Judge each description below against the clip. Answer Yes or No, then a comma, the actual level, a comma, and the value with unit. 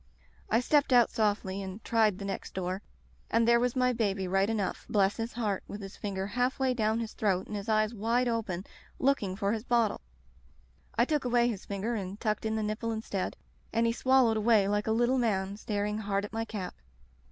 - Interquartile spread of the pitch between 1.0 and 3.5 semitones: Yes, average, 2.8 semitones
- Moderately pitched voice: No, high, 215 Hz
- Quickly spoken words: Yes, fast, 210 wpm